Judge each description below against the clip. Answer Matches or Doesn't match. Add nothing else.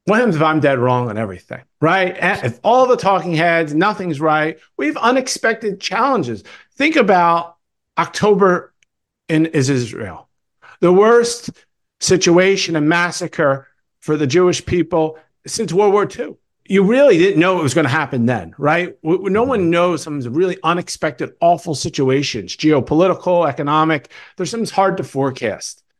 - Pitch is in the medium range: Matches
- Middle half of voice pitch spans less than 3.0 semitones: Doesn't match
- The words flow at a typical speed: Matches